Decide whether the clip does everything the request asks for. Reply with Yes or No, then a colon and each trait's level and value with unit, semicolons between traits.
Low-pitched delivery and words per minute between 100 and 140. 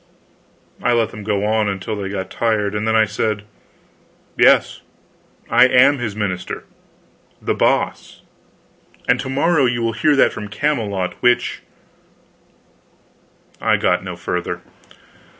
Yes: low, 110 Hz; slow, 135 wpm